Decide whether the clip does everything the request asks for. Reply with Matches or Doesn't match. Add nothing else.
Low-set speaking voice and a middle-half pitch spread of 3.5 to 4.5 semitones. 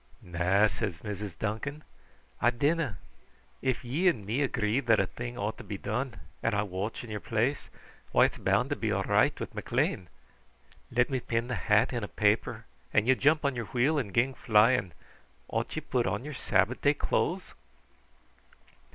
Matches